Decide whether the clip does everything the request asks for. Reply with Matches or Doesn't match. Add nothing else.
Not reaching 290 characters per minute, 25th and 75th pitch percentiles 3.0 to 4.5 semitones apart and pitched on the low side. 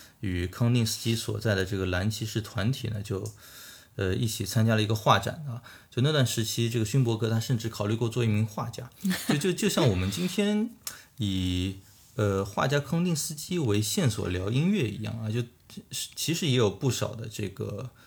Matches